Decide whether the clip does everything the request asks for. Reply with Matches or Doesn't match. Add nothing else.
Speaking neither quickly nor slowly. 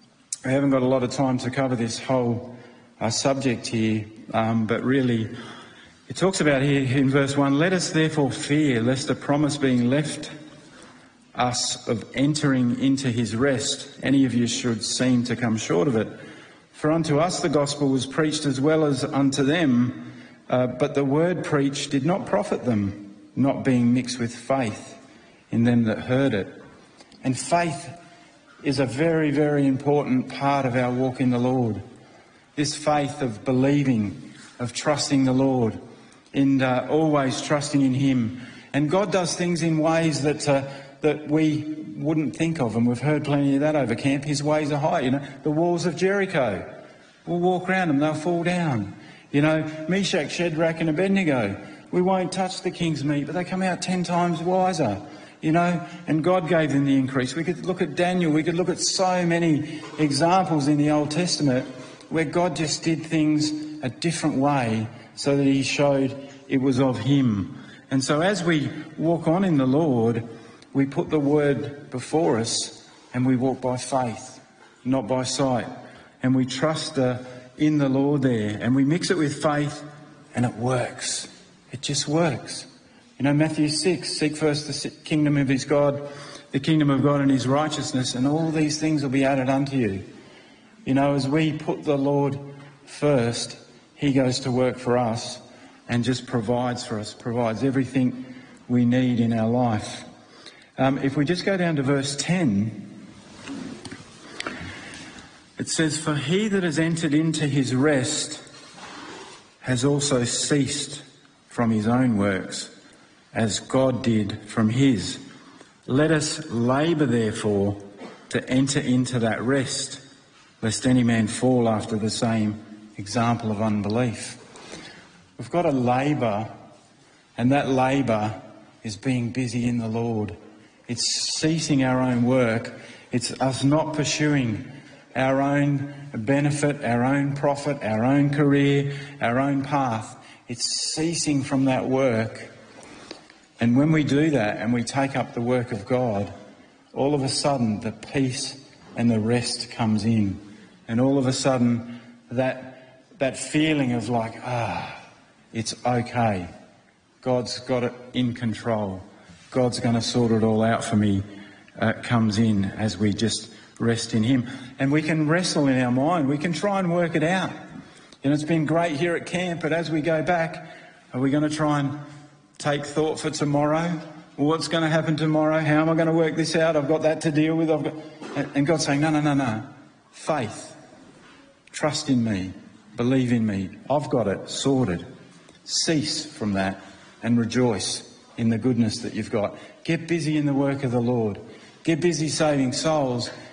Matches